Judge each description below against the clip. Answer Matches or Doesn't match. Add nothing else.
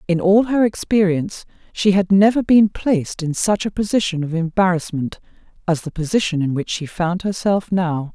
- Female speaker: Matches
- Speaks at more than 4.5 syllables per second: Matches